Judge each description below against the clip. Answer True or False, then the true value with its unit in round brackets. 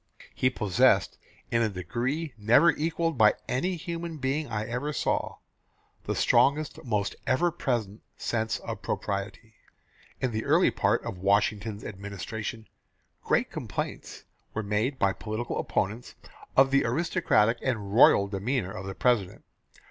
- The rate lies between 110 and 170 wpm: True (135 wpm)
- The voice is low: True (115 Hz)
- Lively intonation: False (4.8 semitones)